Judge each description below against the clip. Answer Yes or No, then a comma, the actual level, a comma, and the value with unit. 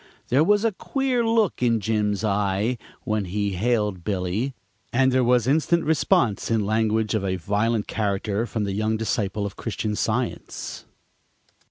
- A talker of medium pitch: No, low, 110 Hz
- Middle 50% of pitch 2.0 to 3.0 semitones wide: No, average, 3.5 semitones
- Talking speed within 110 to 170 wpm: Yes, average, 155 wpm